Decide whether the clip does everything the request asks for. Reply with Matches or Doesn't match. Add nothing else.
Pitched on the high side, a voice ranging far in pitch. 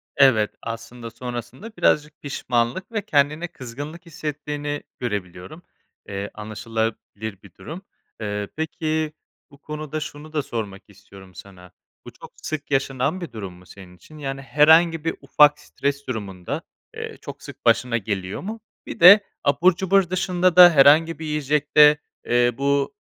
Doesn't match